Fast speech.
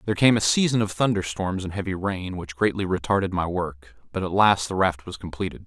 Yes: fast, 235 wpm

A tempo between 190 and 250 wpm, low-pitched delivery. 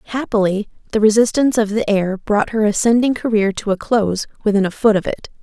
No: average, 200 wpm; high, 210 Hz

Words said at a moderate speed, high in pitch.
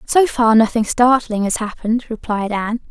Yes: average, 165 wpm; high, 225 Hz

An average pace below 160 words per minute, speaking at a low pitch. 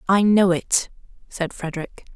No: average, 140 wpm; medium, 185 Hz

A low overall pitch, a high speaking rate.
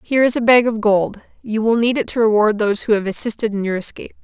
No: high, 220 Hz; fast, 270 wpm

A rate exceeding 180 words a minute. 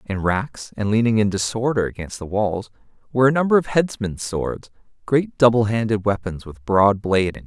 Yes: average, 200 wpm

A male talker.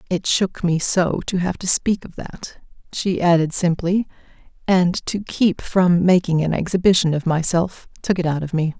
No: female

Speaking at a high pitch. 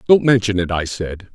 No: low, 105 Hz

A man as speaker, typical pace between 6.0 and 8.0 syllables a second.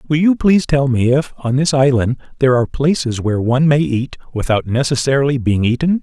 Yes: male; 6.1 syllables/s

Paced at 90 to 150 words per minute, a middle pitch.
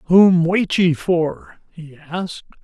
Yes: slow, 135 wpm; medium, 170 Hz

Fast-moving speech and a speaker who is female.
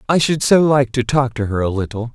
No: fast, 280 wpm; male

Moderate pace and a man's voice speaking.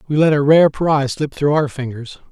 No: fast, 235 wpm; male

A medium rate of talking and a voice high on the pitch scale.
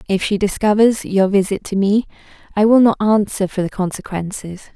Yes: average, 175 wpm; high, 200 Hz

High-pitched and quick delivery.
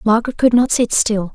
Yes: high, 225 Hz; fast, 225 wpm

